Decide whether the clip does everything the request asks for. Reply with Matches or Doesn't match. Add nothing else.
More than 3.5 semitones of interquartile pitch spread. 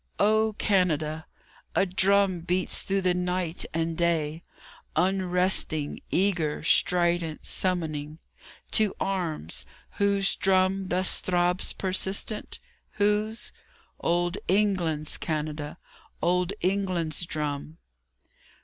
Doesn't match